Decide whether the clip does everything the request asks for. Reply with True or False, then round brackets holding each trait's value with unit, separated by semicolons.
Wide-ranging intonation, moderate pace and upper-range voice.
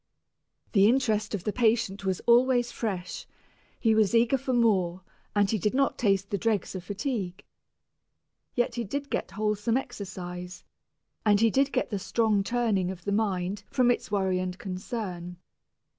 False (3.8 semitones; 165 wpm; 210 Hz)